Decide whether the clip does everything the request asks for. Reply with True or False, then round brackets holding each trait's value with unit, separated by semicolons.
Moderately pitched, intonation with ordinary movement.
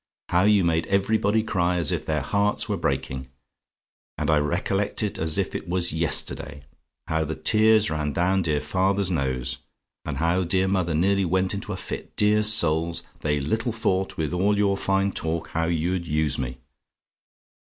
False (85 Hz; 4.1 semitones)